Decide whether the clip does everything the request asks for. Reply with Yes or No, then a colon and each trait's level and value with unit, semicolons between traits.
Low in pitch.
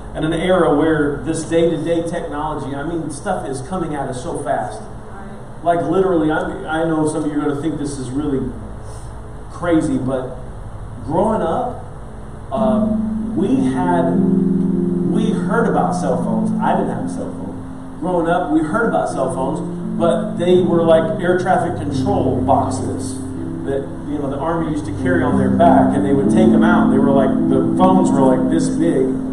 No: medium, 160 Hz